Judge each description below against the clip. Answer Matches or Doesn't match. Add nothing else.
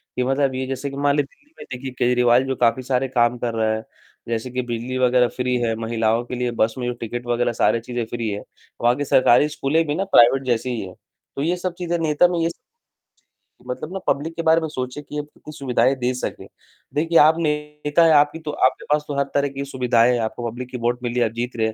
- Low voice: Matches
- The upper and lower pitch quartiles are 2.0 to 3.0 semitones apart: Doesn't match